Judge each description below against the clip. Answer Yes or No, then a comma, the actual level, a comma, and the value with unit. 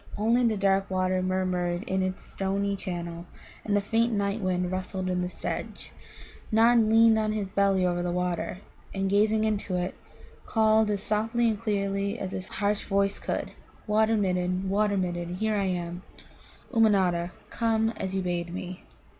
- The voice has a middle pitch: No, high, 195 Hz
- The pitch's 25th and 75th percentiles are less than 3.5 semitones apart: Yes, average, 2.8 semitones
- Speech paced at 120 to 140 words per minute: No, average, 165 wpm